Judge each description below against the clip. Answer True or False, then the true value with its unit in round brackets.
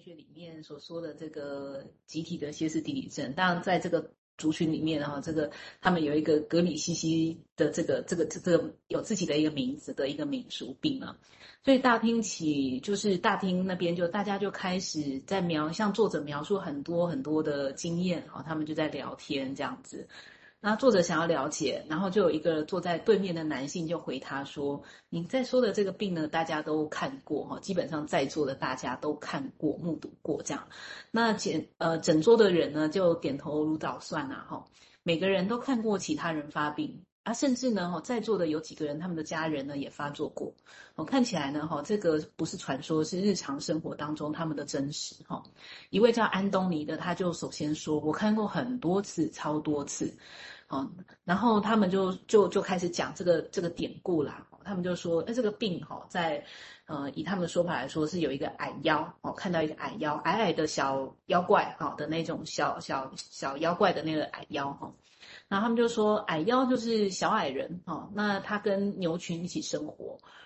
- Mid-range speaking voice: True (170 Hz)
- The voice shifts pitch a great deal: False (4.5 semitones)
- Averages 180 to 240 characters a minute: False (295 characters per minute)